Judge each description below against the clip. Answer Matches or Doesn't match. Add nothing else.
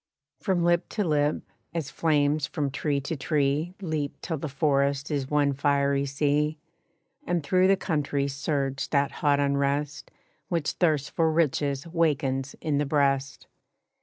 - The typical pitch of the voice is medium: Matches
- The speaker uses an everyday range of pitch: Doesn't match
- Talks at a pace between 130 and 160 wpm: Matches